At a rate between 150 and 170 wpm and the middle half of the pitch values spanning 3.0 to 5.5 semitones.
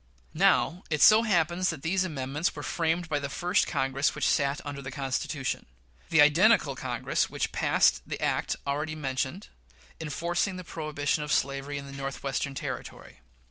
Yes: average, 160 wpm; average, 3.7 semitones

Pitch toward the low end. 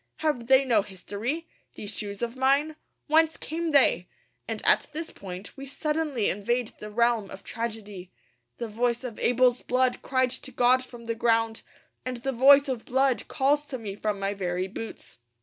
No: high, 240 Hz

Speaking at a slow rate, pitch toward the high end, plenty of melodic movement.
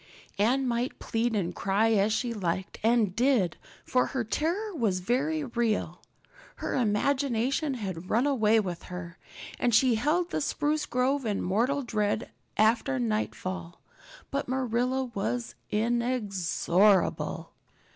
No: slow, 125 wpm; high, 225 Hz; average, 4.9 semitones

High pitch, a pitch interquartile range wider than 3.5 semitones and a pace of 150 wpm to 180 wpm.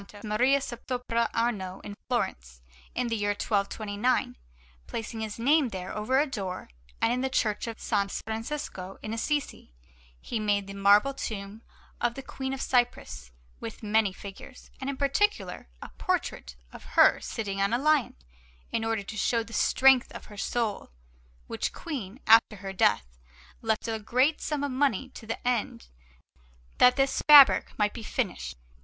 Yes: high, 225 Hz; average, 4.2 semitones; average, 160 wpm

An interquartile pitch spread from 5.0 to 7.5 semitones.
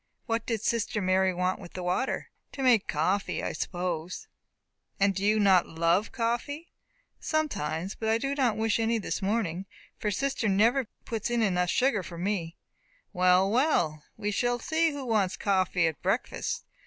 No: average, 4.3 semitones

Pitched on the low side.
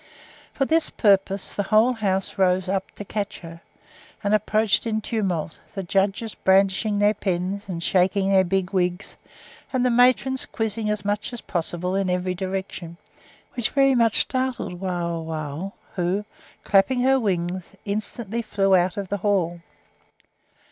No: high, 195 Hz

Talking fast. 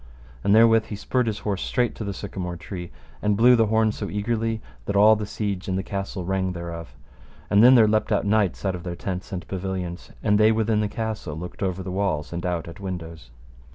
Yes: fast, 225 wpm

